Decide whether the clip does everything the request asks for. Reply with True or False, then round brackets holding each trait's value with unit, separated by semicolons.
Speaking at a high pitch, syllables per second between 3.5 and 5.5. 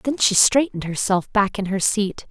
True (210 Hz; 4.9 syllables/s)